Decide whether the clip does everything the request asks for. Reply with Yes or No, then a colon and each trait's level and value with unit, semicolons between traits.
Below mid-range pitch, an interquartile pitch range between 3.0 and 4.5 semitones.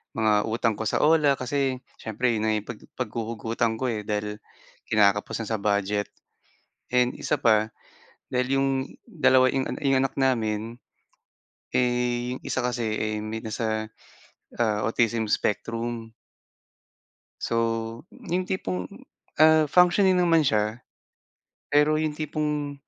Yes: low, 120 Hz; average, 4.0 semitones